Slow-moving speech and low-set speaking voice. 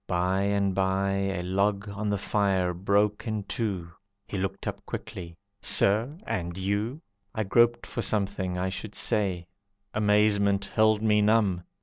No: average, 145 wpm; low, 100 Hz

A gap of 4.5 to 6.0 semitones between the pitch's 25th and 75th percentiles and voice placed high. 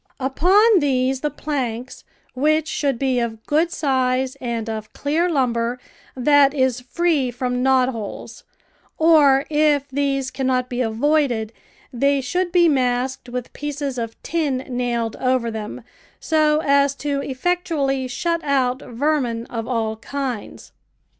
No: average, 3.0 semitones; very high, 265 Hz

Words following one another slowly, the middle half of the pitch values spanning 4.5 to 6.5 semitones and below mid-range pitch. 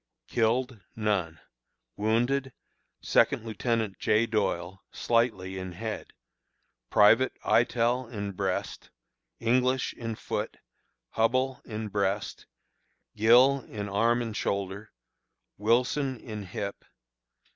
No: slow, 95 wpm; average, 3.1 semitones; low, 110 Hz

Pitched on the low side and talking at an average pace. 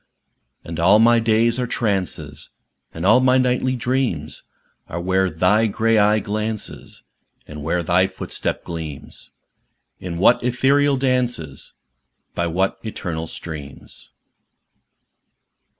No: low, 105 Hz; slow, 115 wpm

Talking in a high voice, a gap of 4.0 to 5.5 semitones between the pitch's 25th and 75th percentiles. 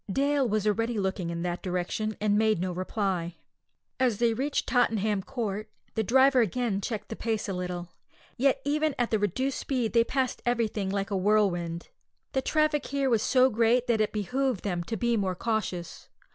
Yes: high, 220 Hz; average, 4.4 semitones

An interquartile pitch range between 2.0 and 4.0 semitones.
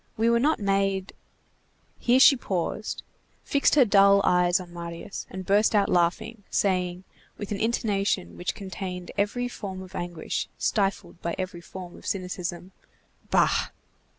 Yes: narrow, 2.6 semitones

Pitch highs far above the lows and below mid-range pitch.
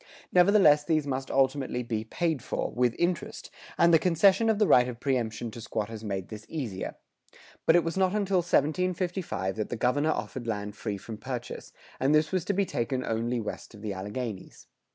Yes: wide, 7.2 semitones; low, 130 Hz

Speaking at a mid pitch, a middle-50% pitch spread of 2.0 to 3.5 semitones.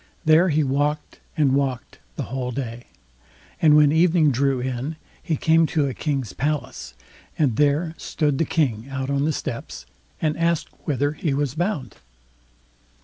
Yes: medium, 145 Hz; average, 2.9 semitones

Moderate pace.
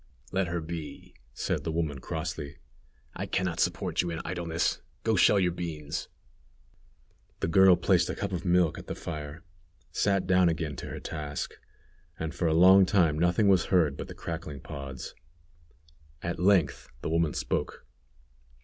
Yes: average, 165 wpm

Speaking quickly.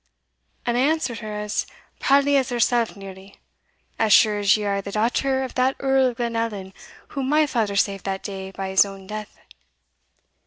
No: average, 180 wpm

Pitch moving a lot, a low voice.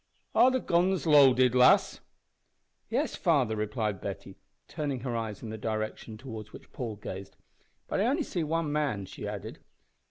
Yes: wide, 6.0 semitones; low, 125 Hz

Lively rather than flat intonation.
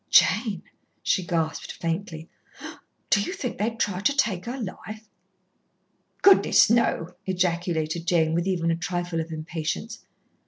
No: average, 4.4 semitones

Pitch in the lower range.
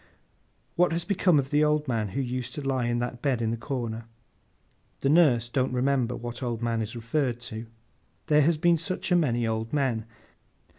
Yes: low, 125 Hz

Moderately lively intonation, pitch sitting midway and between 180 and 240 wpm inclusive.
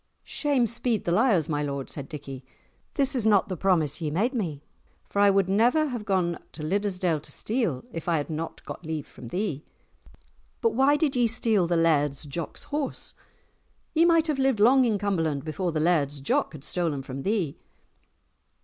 No: wide, 7.3 semitones; medium, 180 Hz; average, 185 wpm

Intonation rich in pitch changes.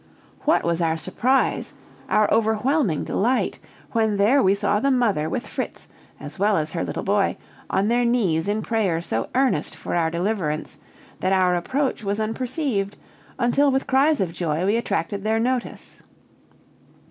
Yes: wide, 5.8 semitones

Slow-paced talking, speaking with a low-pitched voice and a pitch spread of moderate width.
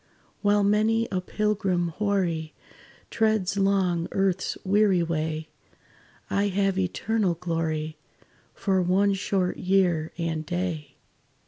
No: slow, 105 wpm; medium, 185 Hz; average, 3.1 semitones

